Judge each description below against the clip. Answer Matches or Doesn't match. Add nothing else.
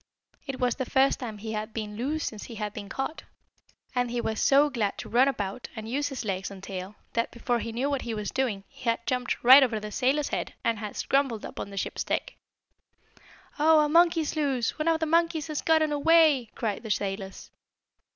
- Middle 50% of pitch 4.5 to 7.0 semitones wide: Matches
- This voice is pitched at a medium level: Doesn't match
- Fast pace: Matches